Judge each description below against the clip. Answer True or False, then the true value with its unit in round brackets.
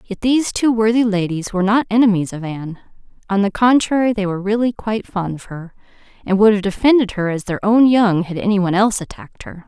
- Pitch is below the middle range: False (205 Hz)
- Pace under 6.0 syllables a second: False (6.2 syllables/s)